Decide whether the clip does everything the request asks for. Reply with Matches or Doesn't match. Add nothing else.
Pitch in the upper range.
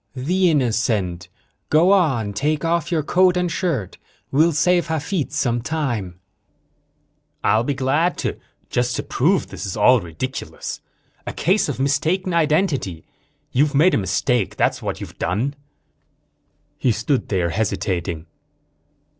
Doesn't match